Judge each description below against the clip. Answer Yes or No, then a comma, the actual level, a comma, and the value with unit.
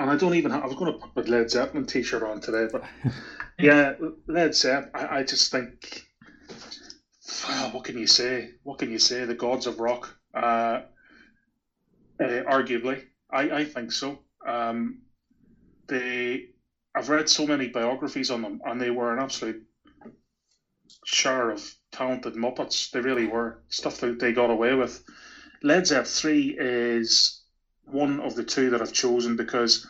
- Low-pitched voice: Yes, low, 125 Hz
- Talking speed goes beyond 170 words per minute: No, average, 165 wpm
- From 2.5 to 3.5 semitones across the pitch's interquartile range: Yes, average, 3.2 semitones